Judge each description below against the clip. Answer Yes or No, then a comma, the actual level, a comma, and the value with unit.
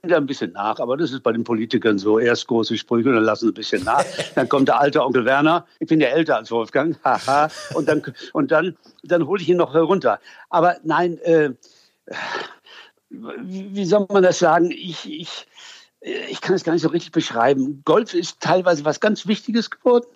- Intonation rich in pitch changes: Yes, wide, 6.3 semitones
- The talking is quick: Yes, fast, 200 wpm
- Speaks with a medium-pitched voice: Yes, medium, 170 Hz